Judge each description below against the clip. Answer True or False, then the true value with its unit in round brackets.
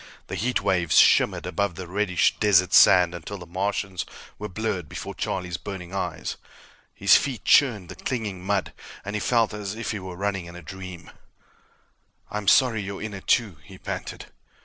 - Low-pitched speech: True (95 Hz)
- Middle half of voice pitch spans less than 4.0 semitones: True (2.6 semitones)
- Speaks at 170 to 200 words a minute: True (175 wpm)